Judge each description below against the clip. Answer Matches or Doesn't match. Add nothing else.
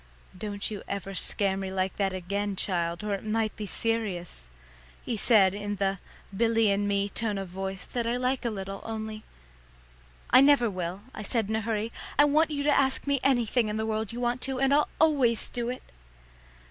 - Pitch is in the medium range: Doesn't match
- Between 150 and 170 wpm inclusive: Doesn't match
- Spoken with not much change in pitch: Doesn't match